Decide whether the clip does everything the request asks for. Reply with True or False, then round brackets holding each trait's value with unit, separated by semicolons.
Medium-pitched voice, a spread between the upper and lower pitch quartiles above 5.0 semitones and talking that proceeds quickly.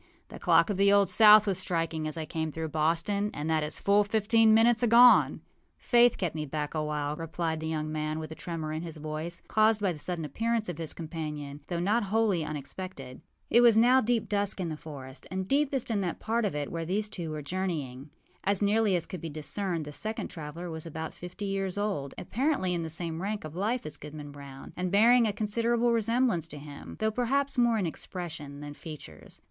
True (175 Hz; 5.6 semitones; 215 wpm)